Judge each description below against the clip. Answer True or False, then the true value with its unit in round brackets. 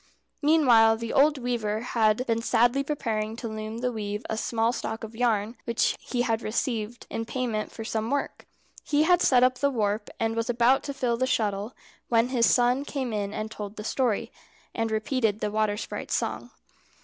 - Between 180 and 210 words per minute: True (190 wpm)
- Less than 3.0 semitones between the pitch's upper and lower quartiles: True (2.5 semitones)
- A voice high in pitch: True (230 Hz)